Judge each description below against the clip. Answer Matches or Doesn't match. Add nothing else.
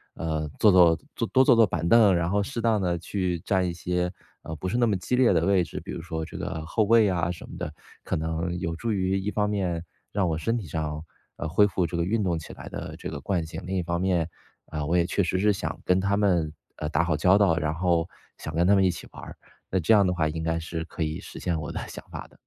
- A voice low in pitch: Matches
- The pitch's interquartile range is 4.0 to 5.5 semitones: Doesn't match